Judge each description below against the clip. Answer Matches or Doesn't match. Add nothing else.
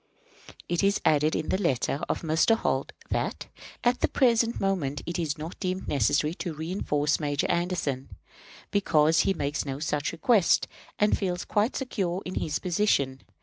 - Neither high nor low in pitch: Matches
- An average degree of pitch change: Matches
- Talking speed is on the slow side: Doesn't match